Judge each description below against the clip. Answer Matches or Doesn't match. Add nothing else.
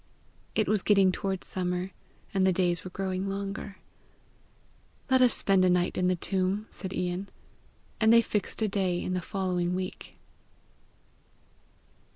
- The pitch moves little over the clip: Matches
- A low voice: Doesn't match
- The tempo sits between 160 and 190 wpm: Doesn't match